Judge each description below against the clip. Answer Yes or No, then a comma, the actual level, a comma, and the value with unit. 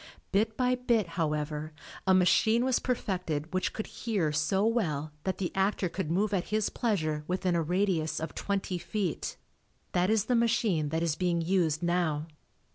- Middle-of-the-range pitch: Yes, medium, 180 Hz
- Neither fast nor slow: Yes, average, 170 wpm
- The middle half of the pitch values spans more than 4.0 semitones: Yes, average, 4.8 semitones